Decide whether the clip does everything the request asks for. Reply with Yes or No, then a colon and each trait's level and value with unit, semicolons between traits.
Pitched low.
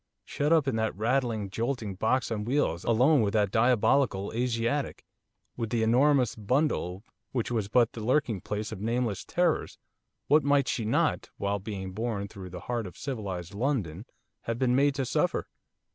Yes: low, 115 Hz